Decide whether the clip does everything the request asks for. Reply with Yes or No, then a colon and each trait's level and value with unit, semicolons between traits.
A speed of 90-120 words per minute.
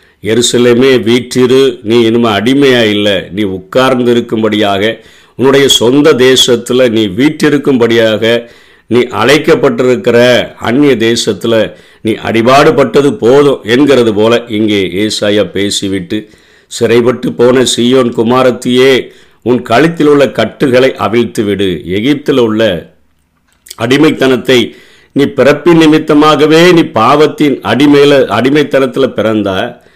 Yes: average, 95 wpm